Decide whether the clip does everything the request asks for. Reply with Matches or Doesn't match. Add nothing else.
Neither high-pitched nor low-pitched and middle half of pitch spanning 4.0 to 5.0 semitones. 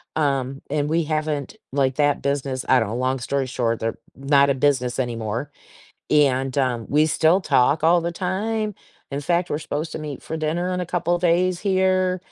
Matches